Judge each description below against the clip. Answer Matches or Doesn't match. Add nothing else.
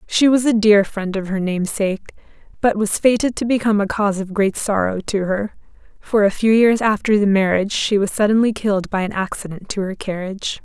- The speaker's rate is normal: Doesn't match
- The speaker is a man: Doesn't match